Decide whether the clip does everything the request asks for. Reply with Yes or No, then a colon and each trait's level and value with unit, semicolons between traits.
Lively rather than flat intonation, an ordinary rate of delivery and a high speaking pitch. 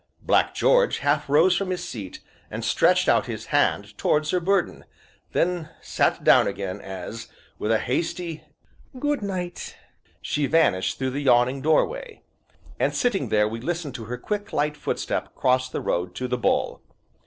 No: wide, 7.4 semitones; average, 165 wpm; medium, 145 Hz